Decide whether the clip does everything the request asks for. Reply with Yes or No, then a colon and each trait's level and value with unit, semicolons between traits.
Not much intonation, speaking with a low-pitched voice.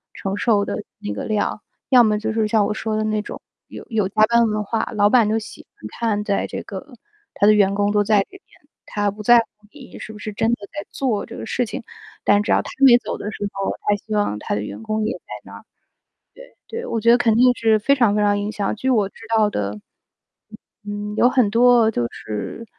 No: narrow, 2.1 semitones; high, 215 Hz